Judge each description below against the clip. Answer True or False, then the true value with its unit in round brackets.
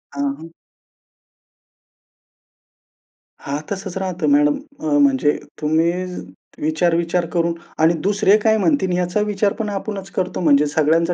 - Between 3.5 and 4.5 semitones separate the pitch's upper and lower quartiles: True (4.1 semitones)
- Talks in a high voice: False (175 Hz)